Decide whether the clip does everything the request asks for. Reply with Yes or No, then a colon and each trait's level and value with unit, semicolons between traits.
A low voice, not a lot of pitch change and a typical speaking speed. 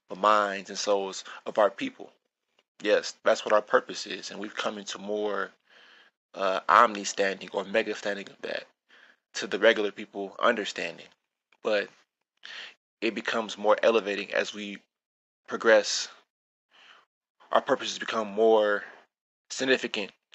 No: low, 105 Hz; narrow, 2.0 semitones; slow, 125 wpm